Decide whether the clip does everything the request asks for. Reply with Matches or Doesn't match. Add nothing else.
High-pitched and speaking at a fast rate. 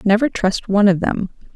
Doesn't match